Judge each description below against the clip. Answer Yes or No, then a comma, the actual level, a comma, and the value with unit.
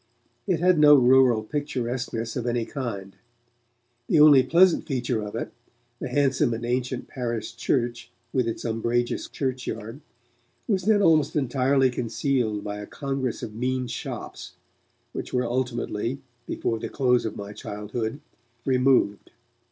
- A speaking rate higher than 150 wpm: No, slow, 135 wpm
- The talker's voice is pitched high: No, low, 125 Hz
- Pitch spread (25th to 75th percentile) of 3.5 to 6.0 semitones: No, average, 3.0 semitones